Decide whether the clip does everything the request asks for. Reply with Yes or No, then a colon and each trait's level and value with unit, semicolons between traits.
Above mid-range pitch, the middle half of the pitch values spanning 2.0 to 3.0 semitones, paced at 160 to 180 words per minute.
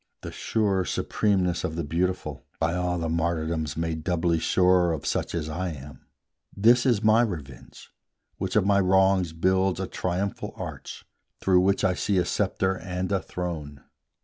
No: very low, 90 Hz; average, 2.7 semitones; average, 165 wpm